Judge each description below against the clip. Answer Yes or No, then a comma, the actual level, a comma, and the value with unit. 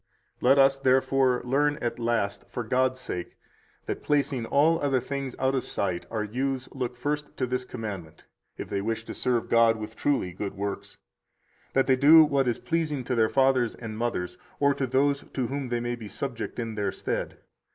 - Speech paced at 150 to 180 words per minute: No, average, 195 wpm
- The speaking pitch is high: No, low, 125 Hz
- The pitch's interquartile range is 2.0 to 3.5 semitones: Yes, average, 3.2 semitones